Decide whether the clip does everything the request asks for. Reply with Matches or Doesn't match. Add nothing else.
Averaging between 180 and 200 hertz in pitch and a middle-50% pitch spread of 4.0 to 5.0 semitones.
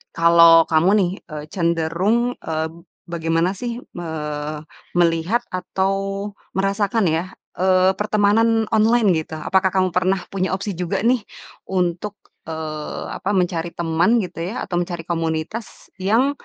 Doesn't match